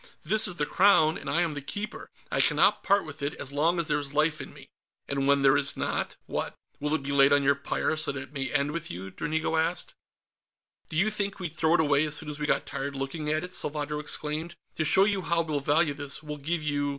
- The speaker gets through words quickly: Yes, fast, 255 wpm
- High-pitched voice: No, medium, 150 Hz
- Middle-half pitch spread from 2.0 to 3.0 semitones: Yes, narrow, 2.5 semitones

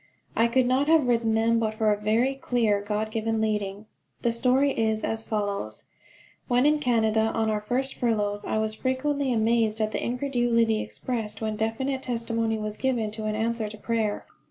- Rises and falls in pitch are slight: Yes, narrow, 2.3 semitones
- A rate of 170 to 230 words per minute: Yes, average, 180 wpm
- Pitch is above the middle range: Yes, high, 225 Hz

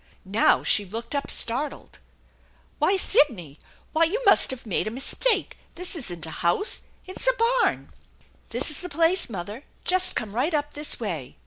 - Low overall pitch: No, very high, 285 Hz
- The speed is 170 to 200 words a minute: Yes, average, 185 wpm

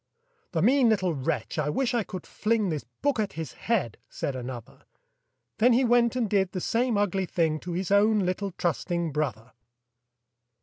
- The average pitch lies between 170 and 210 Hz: Yes, high, 190 Hz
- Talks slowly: No, average, 175 wpm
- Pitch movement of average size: No, wide, 6.5 semitones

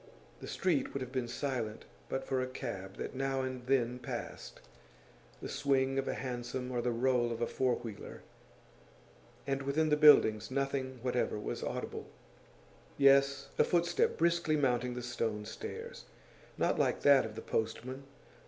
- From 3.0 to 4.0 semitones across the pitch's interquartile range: No, narrow, 2.4 semitones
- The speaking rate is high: No, average, 160 wpm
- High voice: No, low, 130 Hz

